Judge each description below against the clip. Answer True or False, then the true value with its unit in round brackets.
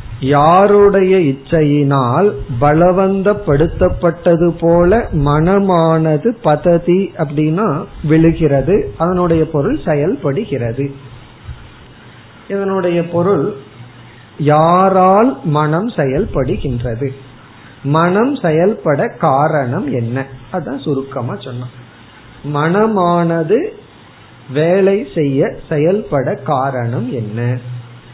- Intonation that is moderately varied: True (5.0 semitones)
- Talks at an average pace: False (60 wpm)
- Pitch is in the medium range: True (155 Hz)